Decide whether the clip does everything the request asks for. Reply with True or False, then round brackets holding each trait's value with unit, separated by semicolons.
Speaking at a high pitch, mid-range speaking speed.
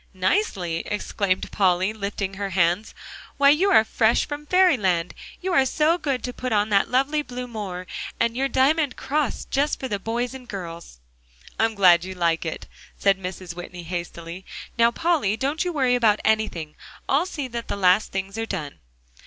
True (220 Hz; 180 wpm)